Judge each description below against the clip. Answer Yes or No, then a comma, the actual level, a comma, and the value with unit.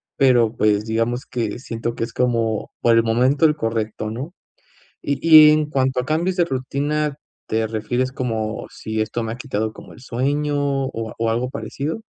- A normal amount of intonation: Yes, average, 3.9 semitones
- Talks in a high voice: No, low, 125 Hz